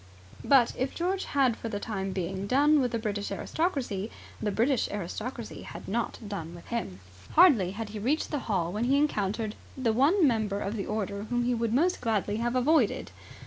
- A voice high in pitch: Yes, high, 225 Hz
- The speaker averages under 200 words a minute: Yes, average, 190 wpm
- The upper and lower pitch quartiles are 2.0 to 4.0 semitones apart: No, average, 4.6 semitones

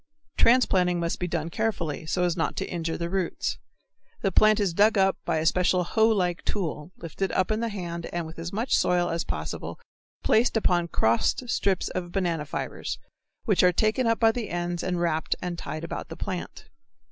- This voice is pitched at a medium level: Yes, medium, 180 Hz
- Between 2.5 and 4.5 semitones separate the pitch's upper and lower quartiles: Yes, average, 3.4 semitones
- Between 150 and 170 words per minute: No, average, 195 wpm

